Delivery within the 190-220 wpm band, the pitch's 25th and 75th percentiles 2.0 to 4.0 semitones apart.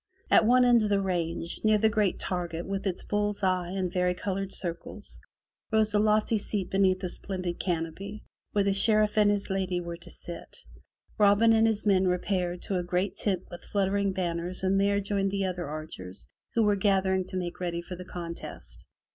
Yes: average, 195 wpm; narrow, 2.4 semitones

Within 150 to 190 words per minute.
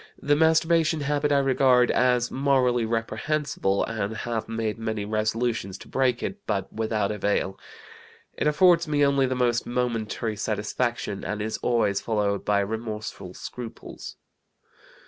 No: slow, 135 wpm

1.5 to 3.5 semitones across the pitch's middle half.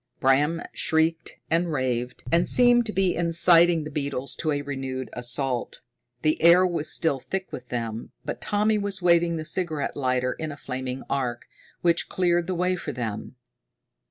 No: average, 4.9 semitones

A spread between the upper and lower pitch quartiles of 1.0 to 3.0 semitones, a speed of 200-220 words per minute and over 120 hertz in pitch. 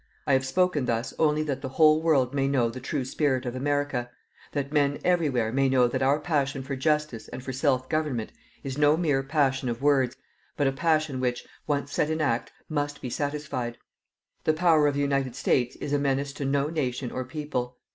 Yes: narrow, 2.5 semitones; fast, 205 wpm; medium, 140 Hz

